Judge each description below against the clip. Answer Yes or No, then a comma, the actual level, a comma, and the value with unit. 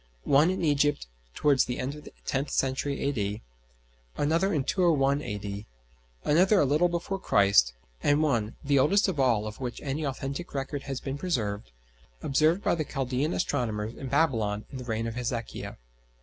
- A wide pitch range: No, average, 4.7 semitones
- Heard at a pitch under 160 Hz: Yes, low, 135 Hz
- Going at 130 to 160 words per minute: No, average, 170 wpm